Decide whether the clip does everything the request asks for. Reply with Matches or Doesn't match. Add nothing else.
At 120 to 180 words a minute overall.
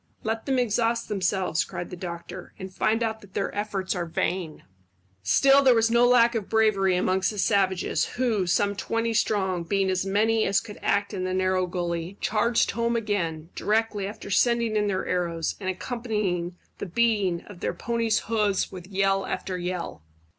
Matches